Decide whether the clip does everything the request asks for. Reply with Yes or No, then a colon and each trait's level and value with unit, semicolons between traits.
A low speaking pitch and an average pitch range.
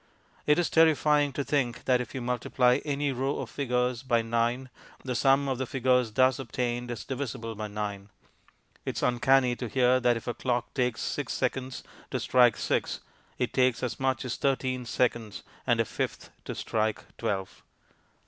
No: low, 125 Hz; narrow, 2.0 semitones